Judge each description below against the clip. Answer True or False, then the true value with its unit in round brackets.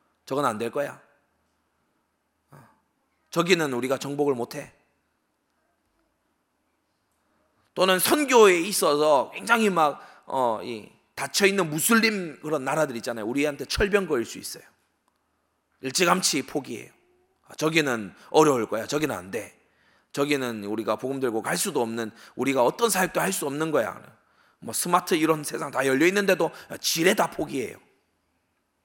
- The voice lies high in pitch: False (145 Hz)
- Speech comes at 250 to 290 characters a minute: True (270 characters per minute)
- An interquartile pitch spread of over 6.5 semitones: True (7.4 semitones)